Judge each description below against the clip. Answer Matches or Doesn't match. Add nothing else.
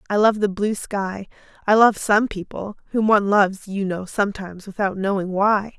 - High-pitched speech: Matches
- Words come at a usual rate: Matches